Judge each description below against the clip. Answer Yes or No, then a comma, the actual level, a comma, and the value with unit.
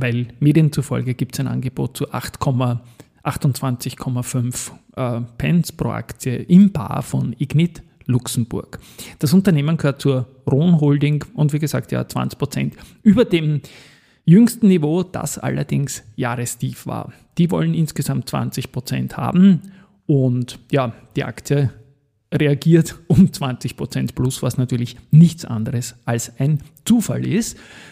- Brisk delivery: No, slow, 125 wpm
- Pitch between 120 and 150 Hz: Yes, low, 135 Hz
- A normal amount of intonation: Yes, average, 3.9 semitones